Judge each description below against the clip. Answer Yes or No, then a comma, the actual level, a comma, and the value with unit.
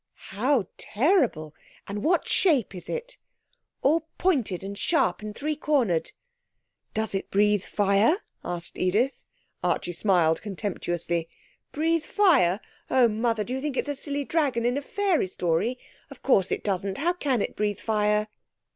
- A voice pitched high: Yes, high, 220 Hz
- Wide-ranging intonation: Yes, wide, 7.0 semitones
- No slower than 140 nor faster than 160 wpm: Yes, average, 150 wpm